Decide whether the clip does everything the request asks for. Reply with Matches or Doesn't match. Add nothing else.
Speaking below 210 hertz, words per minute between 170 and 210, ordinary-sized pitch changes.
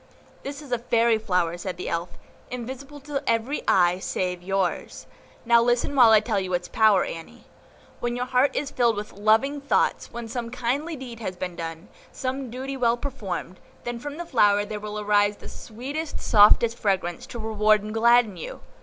Doesn't match